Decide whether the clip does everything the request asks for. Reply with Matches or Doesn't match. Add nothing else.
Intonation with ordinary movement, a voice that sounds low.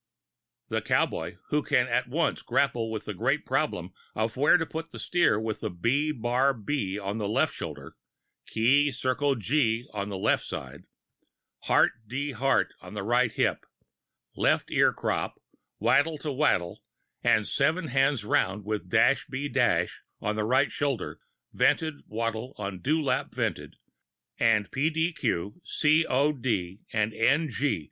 Matches